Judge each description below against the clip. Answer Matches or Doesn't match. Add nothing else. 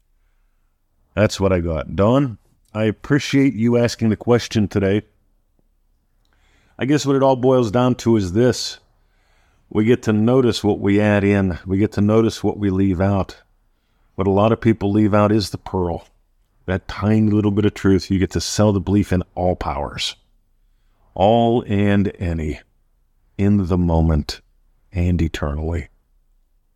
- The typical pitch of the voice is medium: Doesn't match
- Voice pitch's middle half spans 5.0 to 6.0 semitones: Doesn't match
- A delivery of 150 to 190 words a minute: Matches